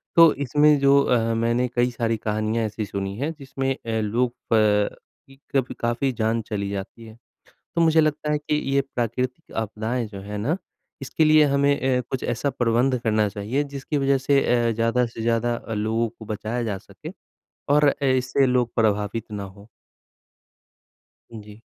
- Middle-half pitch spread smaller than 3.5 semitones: No, average, 3.8 semitones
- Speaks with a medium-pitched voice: No, low, 120 Hz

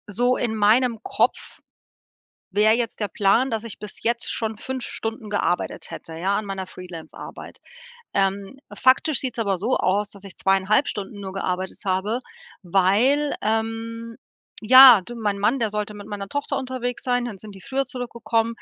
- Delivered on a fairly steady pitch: No, average, 3.5 semitones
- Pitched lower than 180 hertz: No, high, 215 Hz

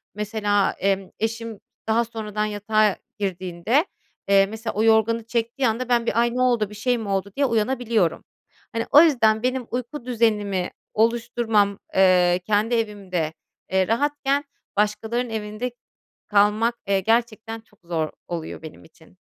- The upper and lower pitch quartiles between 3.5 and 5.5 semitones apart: No, average, 2.7 semitones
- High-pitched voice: Yes, high, 220 Hz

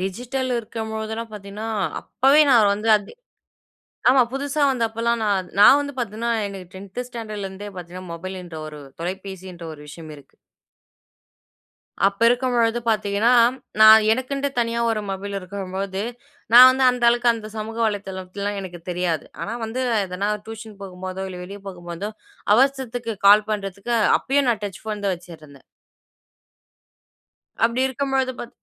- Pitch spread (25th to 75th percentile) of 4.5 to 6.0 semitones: No, average, 3.8 semitones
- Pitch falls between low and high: No, high, 210 Hz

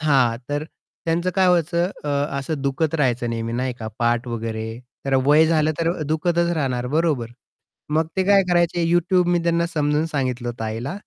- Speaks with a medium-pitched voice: Yes, medium, 150 Hz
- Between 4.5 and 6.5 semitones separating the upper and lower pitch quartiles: Yes, wide, 5.5 semitones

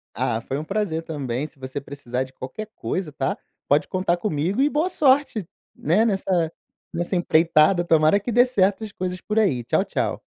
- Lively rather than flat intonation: Yes, wide, 6.1 semitones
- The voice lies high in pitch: No, medium, 175 Hz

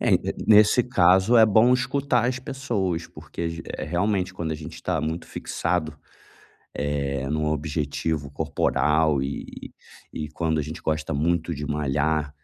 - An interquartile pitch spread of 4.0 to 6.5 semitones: Yes, average, 4.4 semitones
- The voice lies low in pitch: Yes, very low, 80 Hz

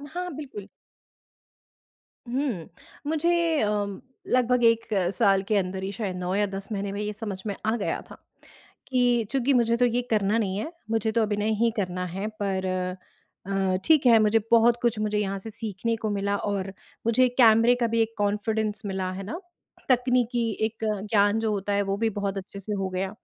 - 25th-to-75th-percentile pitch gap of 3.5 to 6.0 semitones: No, average, 2.9 semitones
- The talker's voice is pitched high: Yes, high, 215 Hz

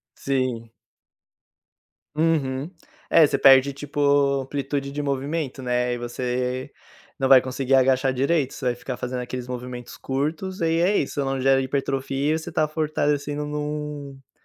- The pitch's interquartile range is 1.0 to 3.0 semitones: Yes, narrow, 2.4 semitones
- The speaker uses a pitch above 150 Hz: No, low, 135 Hz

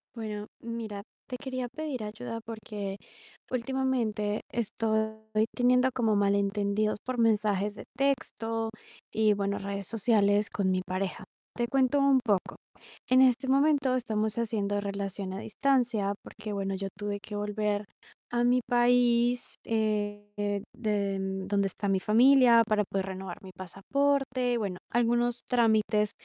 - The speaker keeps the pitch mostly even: No, average, 3.1 semitones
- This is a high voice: Yes, high, 220 Hz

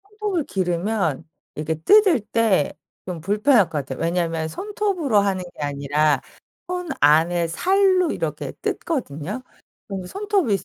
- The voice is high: Yes, high, 195 Hz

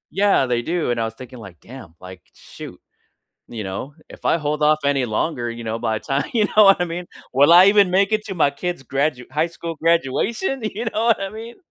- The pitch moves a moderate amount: No, wide, 8.0 semitones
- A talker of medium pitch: Yes, medium, 150 Hz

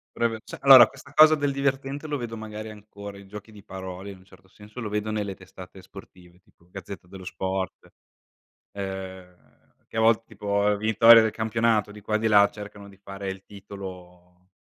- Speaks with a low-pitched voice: Yes, low, 100 Hz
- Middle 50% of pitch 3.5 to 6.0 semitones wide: No, average, 2.7 semitones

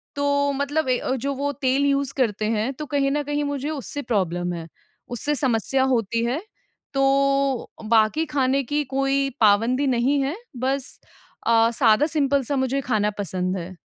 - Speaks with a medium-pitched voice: No, very high, 270 Hz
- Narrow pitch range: No, average, 3.6 semitones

